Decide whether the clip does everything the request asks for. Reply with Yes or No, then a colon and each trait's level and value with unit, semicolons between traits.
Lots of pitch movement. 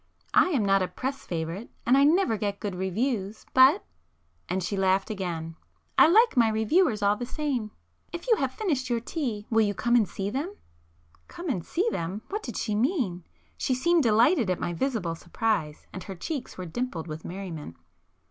Yes: wide, 6.1 semitones